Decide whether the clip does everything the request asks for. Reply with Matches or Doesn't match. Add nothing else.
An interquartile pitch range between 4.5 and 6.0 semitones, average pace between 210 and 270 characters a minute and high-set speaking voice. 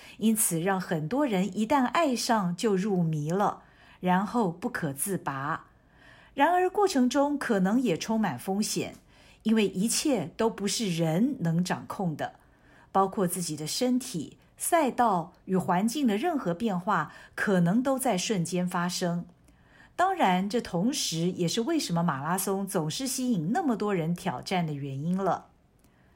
Matches